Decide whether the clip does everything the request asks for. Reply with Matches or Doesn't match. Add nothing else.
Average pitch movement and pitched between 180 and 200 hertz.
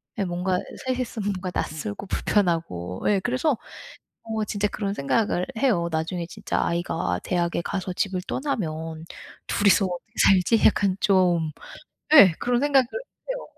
Matches